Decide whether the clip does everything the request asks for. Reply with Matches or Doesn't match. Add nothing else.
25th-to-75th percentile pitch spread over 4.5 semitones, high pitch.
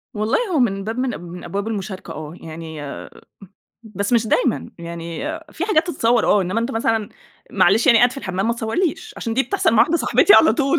Matches